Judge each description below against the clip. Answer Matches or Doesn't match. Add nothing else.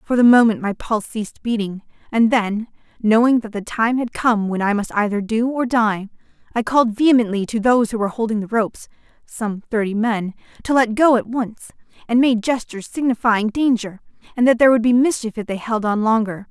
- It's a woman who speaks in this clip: Matches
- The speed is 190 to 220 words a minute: Matches